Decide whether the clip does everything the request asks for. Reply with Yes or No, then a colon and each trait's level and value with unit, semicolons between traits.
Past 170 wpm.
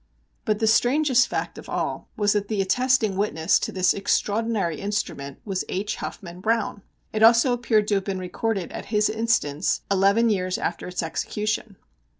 No: average, 165 wpm